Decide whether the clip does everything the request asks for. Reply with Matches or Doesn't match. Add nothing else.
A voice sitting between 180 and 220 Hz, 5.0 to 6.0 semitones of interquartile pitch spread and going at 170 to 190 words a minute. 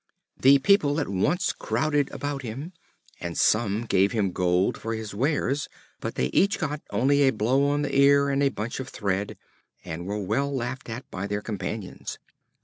Doesn't match